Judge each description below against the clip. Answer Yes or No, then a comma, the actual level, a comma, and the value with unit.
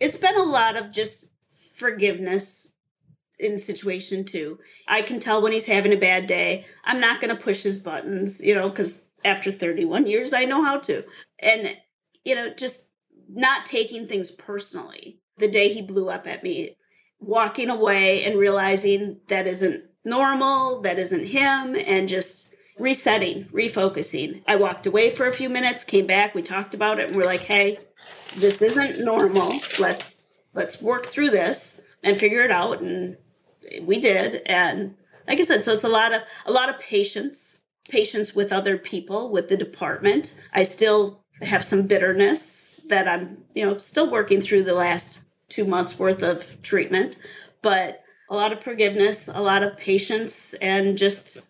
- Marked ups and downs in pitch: No, average, 4.0 semitones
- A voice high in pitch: Yes, high, 205 Hz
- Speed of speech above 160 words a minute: Yes, average, 170 wpm